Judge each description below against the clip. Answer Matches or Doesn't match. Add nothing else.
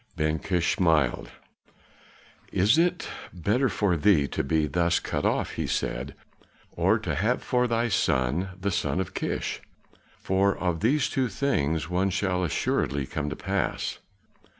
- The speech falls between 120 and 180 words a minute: Matches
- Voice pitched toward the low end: Matches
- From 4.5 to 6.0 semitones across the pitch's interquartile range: Matches